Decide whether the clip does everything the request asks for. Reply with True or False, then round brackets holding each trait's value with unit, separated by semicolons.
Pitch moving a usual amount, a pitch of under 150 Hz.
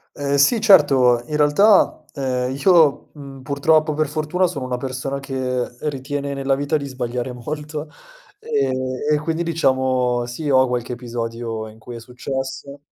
True (3.1 semitones; 135 Hz)